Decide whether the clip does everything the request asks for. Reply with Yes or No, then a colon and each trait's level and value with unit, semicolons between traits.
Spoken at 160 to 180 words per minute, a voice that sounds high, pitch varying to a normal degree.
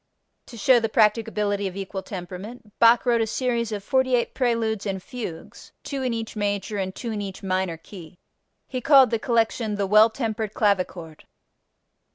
Yes: average, 170 wpm; high, 215 Hz; average, 3.0 semitones